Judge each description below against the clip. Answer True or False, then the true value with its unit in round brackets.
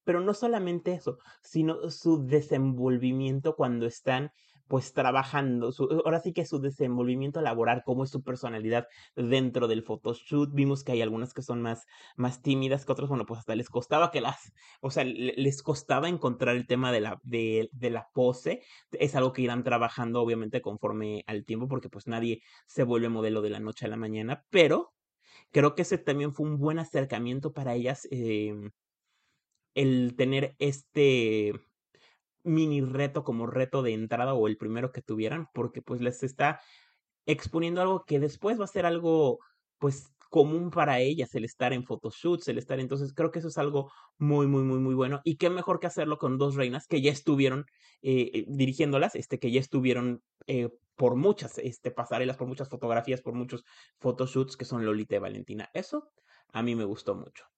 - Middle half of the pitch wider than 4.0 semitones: False (3.5 semitones)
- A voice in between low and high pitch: False (130 Hz)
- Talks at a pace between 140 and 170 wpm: False (180 wpm)